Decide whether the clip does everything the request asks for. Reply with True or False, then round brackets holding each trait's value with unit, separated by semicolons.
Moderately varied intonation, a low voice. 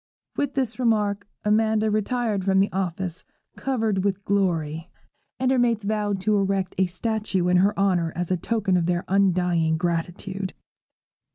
False (3.1 semitones; 195 Hz)